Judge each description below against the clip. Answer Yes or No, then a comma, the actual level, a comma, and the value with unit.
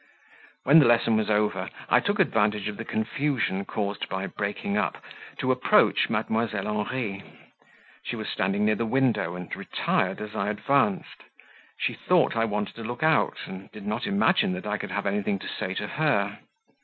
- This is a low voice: Yes, low, 105 Hz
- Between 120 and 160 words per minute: No, average, 180 wpm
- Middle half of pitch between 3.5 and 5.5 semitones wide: No, average, 2.7 semitones